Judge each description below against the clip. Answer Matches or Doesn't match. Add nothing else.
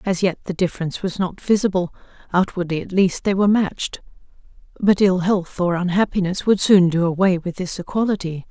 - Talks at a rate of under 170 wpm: Doesn't match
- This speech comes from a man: Doesn't match